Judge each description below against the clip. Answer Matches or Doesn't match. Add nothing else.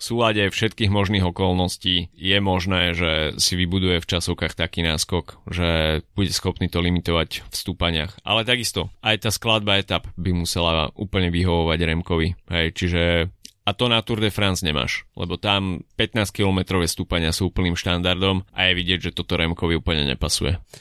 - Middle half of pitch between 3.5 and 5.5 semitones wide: Doesn't match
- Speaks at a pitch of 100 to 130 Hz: Doesn't match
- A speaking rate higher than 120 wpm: Matches